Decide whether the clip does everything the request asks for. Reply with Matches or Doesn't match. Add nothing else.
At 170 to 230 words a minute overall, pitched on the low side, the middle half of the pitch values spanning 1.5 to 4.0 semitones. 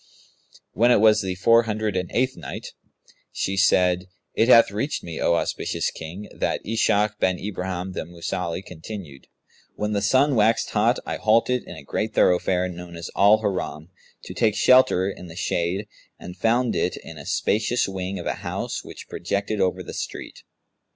Matches